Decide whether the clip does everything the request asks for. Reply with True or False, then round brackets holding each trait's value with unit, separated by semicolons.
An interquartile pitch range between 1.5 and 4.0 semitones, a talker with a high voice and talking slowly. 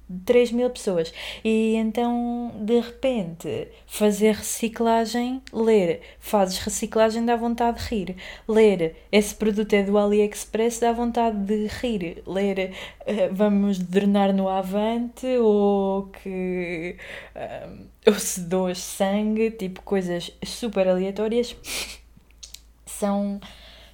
True (3.0 semitones; 210 Hz; 105 wpm)